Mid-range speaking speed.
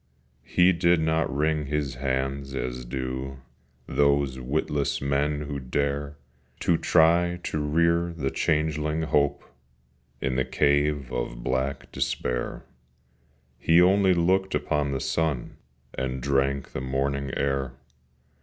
No: slow, 120 wpm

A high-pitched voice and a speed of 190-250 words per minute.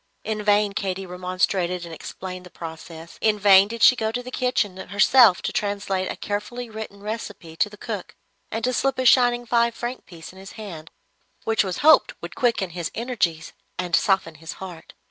Yes: high, 205 Hz; average, 195 wpm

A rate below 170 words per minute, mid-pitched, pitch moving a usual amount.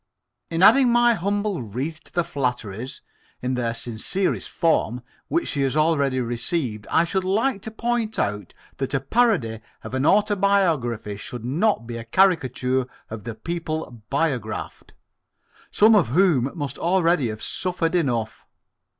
No: average, 145 wpm; medium, 145 Hz; wide, 7.8 semitones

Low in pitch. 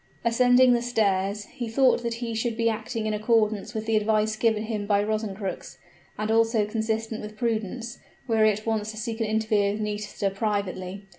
No: high, 220 Hz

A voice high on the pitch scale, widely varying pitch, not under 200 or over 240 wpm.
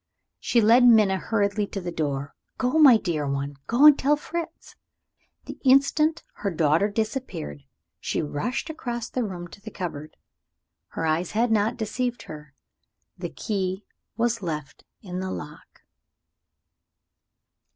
No: high, 205 Hz; wide, 7.2 semitones; average, 140 wpm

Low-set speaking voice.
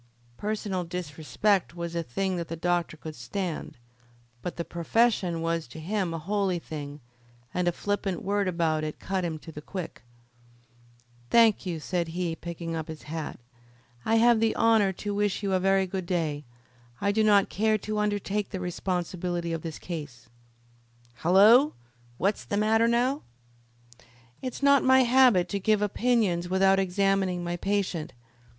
No: medium, 185 Hz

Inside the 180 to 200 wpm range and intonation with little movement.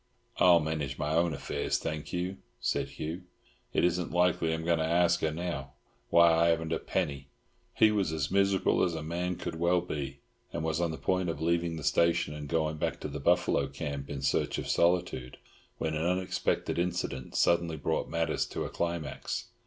Yes: average, 195 wpm; narrow, 2.2 semitones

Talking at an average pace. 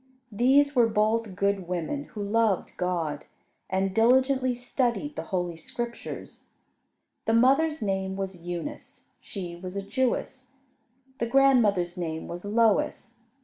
No: slow, 125 wpm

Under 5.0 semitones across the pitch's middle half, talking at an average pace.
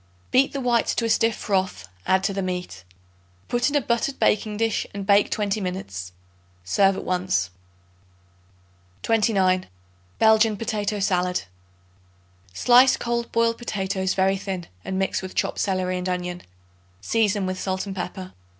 Yes: average, 3.3 semitones; average, 150 wpm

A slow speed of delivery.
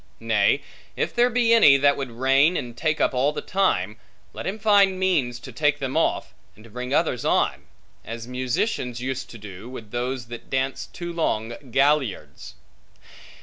No: average, 175 wpm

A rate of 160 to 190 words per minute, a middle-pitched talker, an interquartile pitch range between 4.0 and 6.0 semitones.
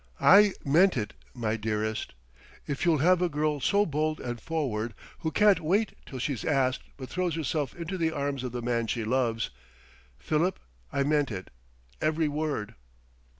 Yes: average, 165 wpm; medium, 145 Hz; average, 5.2 semitones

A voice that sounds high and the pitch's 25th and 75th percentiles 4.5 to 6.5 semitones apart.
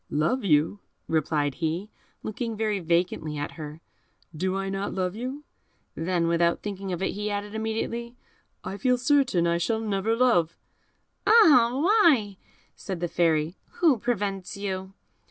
Yes: high, 195 Hz; average, 5.2 semitones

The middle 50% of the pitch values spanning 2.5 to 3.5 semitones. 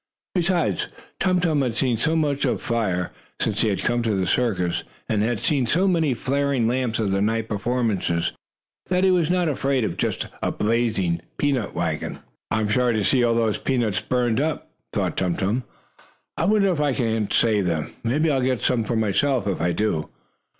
No: average, 5.1 semitones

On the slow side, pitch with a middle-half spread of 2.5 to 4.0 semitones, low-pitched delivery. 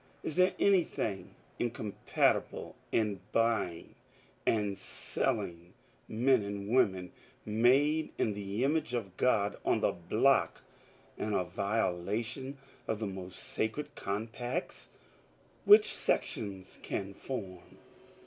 No: slow, 110 wpm; average, 4.5 semitones; low, 110 Hz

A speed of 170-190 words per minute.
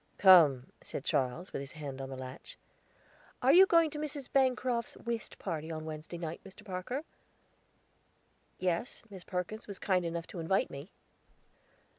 No: average, 155 wpm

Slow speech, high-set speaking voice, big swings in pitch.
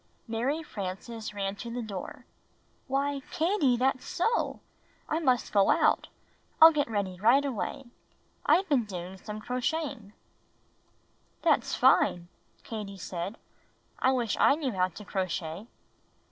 Yes: slow, 130 wpm; high, 230 Hz; wide, 5.8 semitones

